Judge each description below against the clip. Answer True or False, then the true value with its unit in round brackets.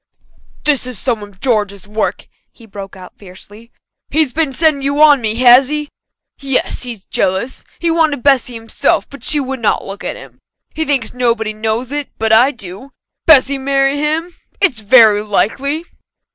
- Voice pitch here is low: False (250 Hz)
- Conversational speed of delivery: True (170 wpm)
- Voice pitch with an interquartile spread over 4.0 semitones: True (4.6 semitones)